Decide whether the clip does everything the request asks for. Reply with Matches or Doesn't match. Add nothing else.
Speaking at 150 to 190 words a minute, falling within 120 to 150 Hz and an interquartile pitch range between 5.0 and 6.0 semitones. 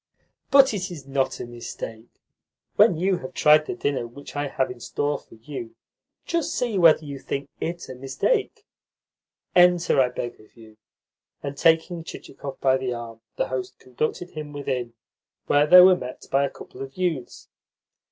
Matches